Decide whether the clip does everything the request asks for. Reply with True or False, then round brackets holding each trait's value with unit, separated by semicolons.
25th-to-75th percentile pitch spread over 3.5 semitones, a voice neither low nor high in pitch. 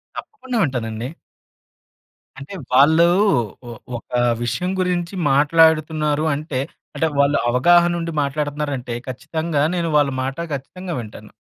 True (3.9 semitones; 150 Hz)